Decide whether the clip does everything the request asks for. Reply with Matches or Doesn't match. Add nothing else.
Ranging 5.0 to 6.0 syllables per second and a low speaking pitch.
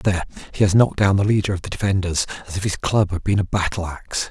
Doesn't match